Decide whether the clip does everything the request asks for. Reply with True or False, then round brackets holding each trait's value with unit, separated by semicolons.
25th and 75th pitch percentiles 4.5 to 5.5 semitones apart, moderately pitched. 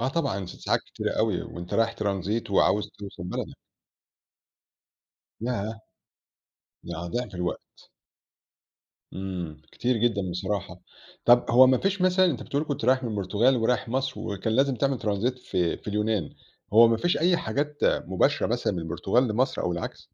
False (5.1 semitones; 110 Hz)